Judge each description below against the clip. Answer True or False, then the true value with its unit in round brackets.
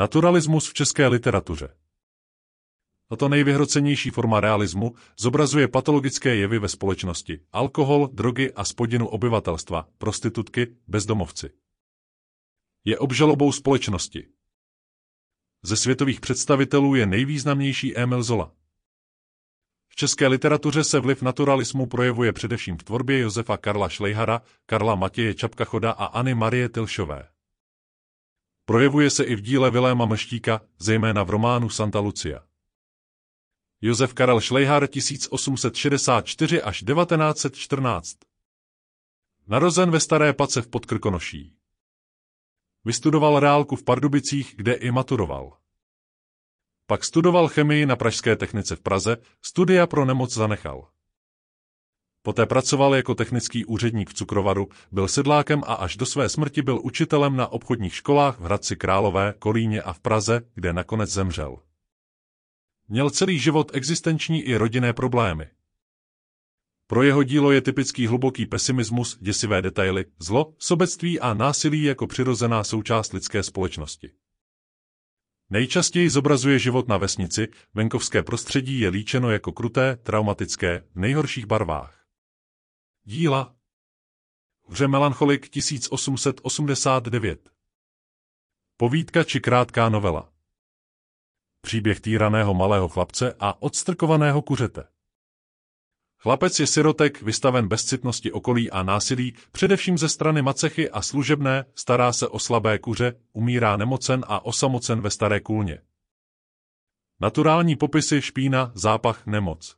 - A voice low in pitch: True (115 Hz)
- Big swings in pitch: True (5.9 semitones)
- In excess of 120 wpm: False (115 wpm)